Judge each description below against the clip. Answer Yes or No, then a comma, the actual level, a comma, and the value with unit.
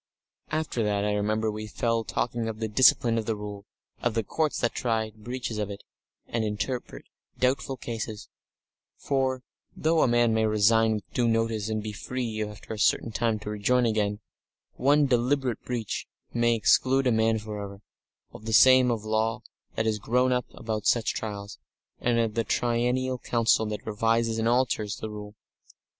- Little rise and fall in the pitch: Yes, narrow, 2.3 semitones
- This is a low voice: Yes, low, 115 Hz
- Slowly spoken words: No, average, 180 wpm